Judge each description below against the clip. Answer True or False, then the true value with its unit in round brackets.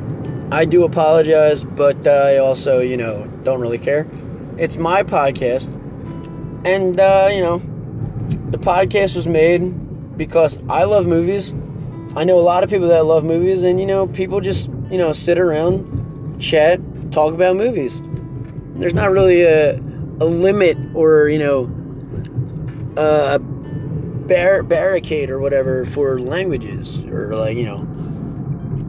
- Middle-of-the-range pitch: True (150 Hz)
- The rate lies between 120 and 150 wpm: True (145 wpm)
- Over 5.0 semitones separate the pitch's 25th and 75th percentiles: False (3.7 semitones)